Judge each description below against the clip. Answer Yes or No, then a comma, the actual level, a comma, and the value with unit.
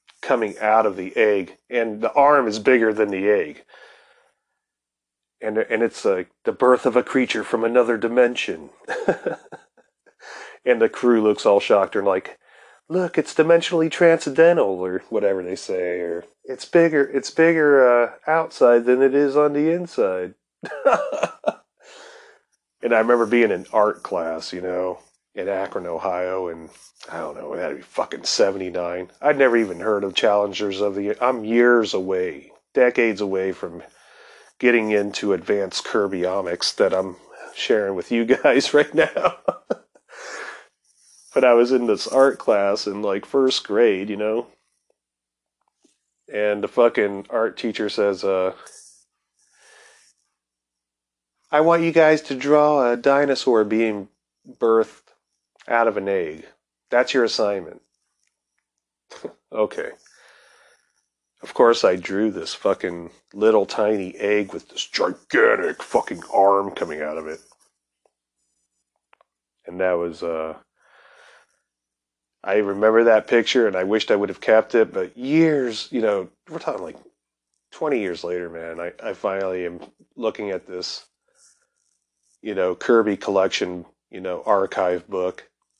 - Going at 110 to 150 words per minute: Yes, average, 140 wpm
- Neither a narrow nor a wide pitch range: No, wide, 6.0 semitones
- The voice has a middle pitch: No, low, 105 Hz